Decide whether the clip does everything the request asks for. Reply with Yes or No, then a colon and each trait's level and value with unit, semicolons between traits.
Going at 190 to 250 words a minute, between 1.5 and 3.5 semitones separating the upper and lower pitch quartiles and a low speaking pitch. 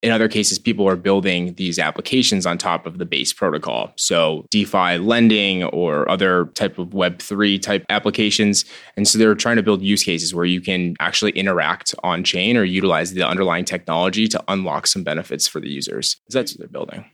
Yes: average, 195 wpm; average, 2.8 semitones; low, 100 Hz